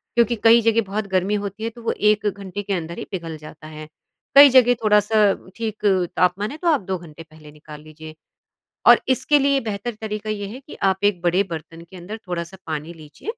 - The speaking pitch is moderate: No, high, 200 Hz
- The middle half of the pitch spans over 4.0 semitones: Yes, average, 4.9 semitones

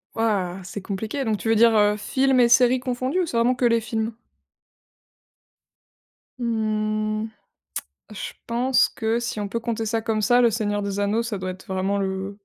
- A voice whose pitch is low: No, high, 220 Hz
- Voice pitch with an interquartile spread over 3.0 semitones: No, narrow, 2.5 semitones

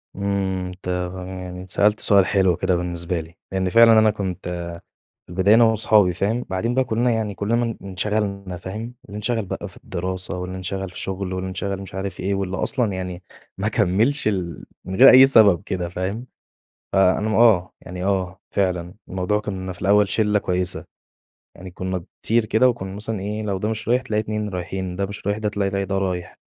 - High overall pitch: No, very low, 95 Hz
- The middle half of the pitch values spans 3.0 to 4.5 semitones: No, narrow, 2.5 semitones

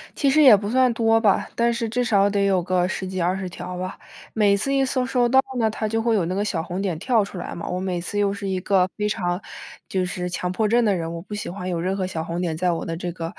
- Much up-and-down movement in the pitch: No, average, 3.8 semitones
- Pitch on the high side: Yes, high, 195 Hz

